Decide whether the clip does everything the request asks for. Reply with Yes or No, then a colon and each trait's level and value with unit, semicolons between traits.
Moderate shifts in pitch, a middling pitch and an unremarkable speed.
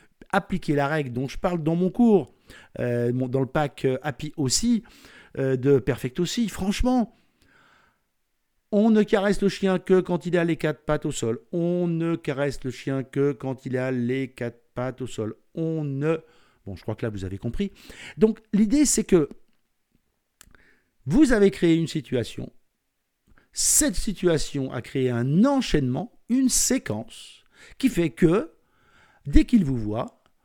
No: wide, 7.2 semitones; medium, 160 Hz; average, 165 wpm